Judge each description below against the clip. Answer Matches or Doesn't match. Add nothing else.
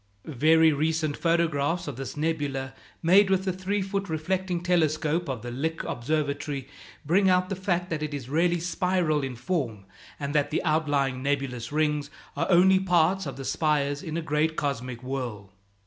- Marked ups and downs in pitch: Doesn't match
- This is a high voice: Doesn't match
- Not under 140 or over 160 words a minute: Doesn't match